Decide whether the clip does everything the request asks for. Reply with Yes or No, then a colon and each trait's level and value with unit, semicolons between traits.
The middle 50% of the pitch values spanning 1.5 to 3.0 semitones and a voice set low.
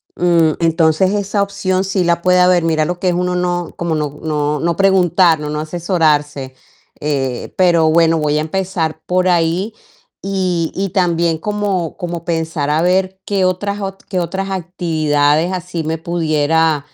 No: average, 2.7 semitones; medium, 170 Hz